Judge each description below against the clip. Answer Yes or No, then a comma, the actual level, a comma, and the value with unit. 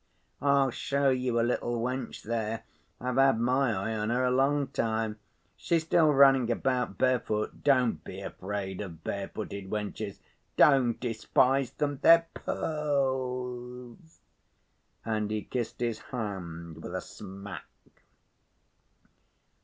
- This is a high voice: No, low, 120 Hz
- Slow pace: Yes, slow, 115 wpm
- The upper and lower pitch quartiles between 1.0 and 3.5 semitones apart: No, average, 3.9 semitones